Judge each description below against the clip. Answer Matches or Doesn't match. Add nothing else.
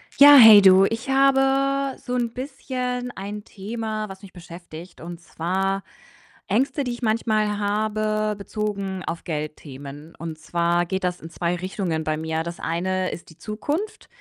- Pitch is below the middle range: Doesn't match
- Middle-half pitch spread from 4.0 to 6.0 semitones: Matches